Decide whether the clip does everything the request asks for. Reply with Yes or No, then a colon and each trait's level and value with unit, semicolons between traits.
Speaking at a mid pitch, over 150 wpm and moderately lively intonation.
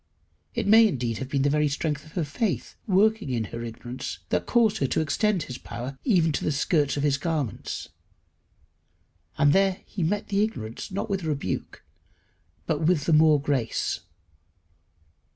No: medium, 150 Hz; average, 170 wpm; wide, 5.8 semitones